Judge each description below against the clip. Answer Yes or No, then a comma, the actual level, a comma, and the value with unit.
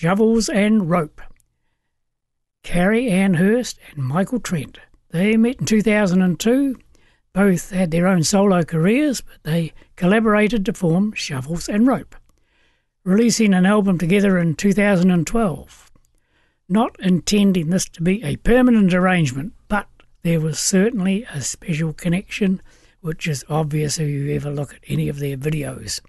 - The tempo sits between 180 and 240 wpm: No, average, 140 wpm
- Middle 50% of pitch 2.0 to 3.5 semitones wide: No, average, 4.5 semitones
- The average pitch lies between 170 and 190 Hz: Yes, medium, 185 Hz